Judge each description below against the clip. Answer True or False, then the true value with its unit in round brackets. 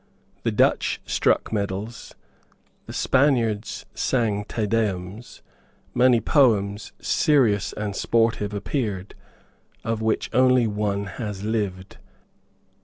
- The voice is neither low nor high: False (110 Hz)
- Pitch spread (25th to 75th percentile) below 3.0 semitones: True (2.6 semitones)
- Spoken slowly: True (100 wpm)